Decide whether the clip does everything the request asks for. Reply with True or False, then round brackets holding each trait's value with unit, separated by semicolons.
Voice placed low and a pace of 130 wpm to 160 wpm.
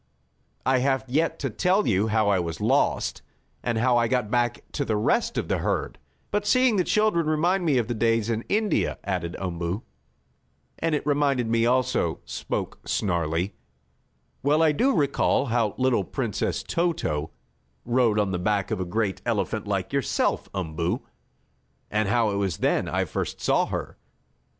False (115 Hz; 170 wpm)